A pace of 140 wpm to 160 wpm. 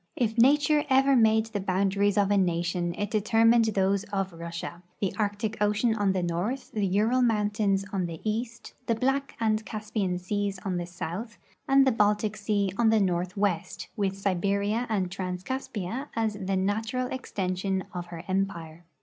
No: average, 170 wpm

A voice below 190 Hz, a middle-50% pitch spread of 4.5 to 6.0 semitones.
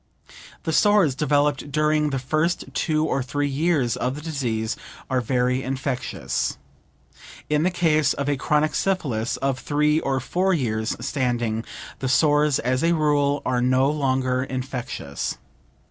No: medium, 140 Hz; average, 3.0 semitones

